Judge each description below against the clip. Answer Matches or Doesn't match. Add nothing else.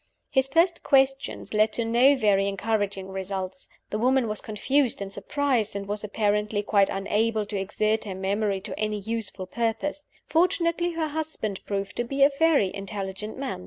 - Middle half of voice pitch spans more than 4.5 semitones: Matches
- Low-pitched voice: Doesn't match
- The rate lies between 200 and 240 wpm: Doesn't match